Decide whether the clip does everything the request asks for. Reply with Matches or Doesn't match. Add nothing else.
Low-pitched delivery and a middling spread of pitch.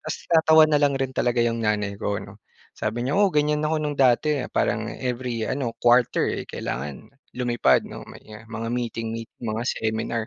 Matches